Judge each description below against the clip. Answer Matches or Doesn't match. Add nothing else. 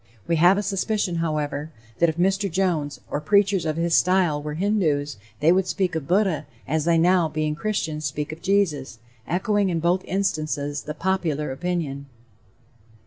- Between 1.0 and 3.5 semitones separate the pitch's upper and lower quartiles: Doesn't match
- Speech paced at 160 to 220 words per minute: Matches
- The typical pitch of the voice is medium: Matches